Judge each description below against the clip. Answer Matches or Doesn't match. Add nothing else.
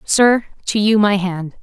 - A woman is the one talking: Matches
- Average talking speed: Matches